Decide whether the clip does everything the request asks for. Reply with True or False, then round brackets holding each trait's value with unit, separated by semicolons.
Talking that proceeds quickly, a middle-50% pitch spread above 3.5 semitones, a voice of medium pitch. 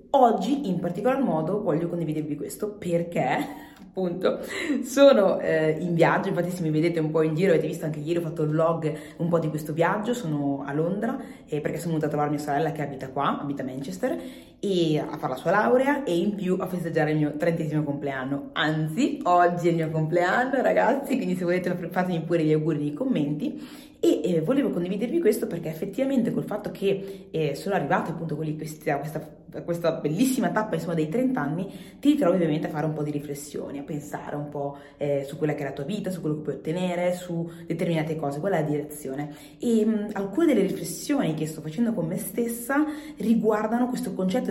True (205 wpm; 5.3 semitones; 170 Hz)